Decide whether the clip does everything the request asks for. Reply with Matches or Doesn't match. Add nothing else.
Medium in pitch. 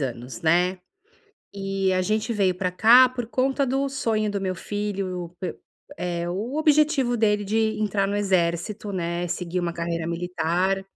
Doesn't match